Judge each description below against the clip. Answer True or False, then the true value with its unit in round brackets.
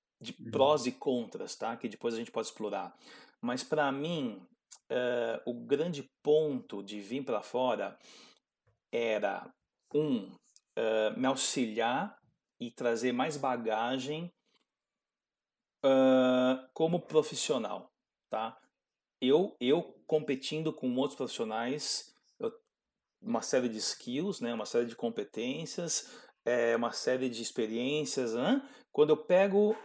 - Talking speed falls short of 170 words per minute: True (120 wpm)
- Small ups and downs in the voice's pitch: False (4.7 semitones)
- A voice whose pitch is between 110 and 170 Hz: True (135 Hz)